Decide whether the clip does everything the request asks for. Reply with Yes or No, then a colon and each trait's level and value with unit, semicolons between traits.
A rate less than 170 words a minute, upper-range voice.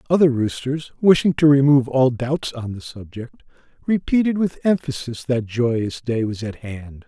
No: average, 160 wpm; low, 130 Hz